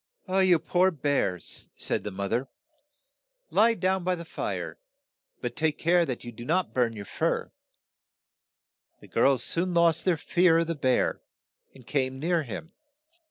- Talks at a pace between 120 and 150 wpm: No, average, 160 wpm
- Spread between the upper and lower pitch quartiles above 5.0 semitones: Yes, wide, 5.5 semitones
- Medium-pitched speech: Yes, medium, 160 Hz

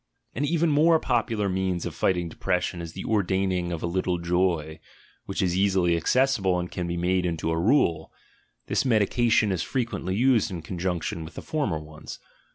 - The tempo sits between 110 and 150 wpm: No, average, 175 wpm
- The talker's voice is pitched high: No, very low, 95 Hz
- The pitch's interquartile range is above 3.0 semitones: Yes, average, 4.1 semitones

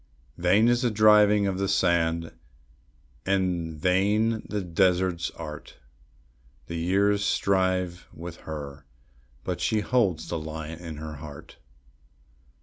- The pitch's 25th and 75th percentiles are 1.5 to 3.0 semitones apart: No, average, 3.6 semitones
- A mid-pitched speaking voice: No, very low, 90 Hz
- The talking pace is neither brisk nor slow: No, slow, 120 wpm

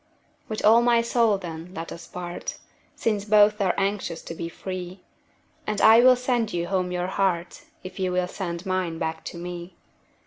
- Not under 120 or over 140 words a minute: No, average, 180 wpm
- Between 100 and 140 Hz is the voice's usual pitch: No, medium, 185 Hz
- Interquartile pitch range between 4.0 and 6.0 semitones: No, average, 3.3 semitones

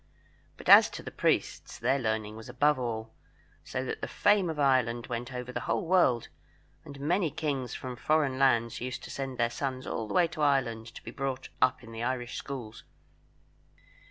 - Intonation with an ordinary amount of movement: Yes, average, 3.2 semitones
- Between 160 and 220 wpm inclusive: Yes, average, 190 wpm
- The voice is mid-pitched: No, low, 130 Hz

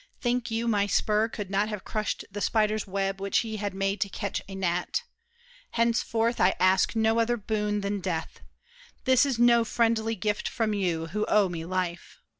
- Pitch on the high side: Yes, high, 210 Hz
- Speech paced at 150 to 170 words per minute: No, average, 185 wpm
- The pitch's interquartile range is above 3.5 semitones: No, average, 2.7 semitones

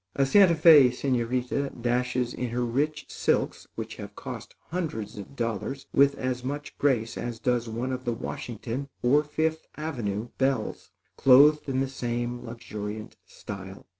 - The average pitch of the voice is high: No, low, 125 Hz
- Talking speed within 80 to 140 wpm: No, average, 150 wpm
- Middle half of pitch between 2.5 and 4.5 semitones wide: Yes, average, 3.1 semitones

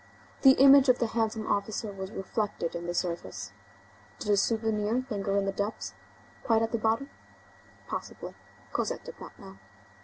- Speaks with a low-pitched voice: No, high, 215 Hz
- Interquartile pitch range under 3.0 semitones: Yes, narrow, 2.6 semitones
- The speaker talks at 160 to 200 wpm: No, average, 150 wpm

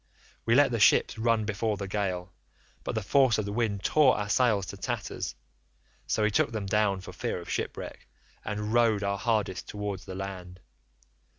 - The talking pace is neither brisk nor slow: Yes, average, 185 wpm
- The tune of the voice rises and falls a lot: No, narrow, 2.6 semitones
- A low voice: Yes, low, 105 Hz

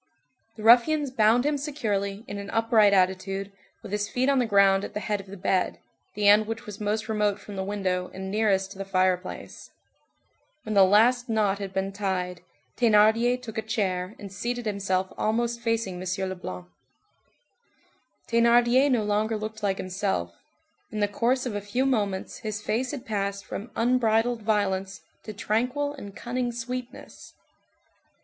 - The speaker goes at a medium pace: Yes, average, 165 wpm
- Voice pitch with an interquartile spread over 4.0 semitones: No, average, 3.2 semitones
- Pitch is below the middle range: No, high, 210 Hz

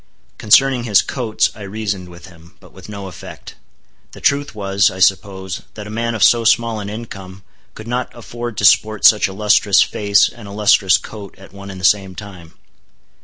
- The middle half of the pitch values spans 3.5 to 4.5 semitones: No, narrow, 2.4 semitones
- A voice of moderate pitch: No, low, 100 Hz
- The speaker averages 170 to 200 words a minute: Yes, average, 195 wpm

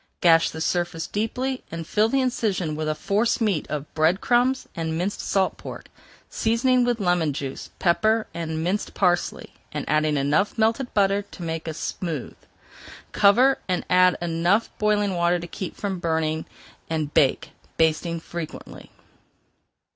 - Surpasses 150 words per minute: No, average, 145 wpm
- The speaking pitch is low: No, medium, 175 Hz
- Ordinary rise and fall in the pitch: Yes, average, 4.7 semitones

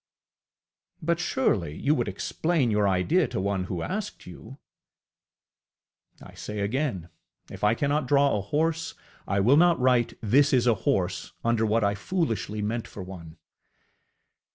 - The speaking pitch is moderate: No, low, 115 Hz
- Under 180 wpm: Yes, average, 150 wpm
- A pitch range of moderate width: No, wide, 6.4 semitones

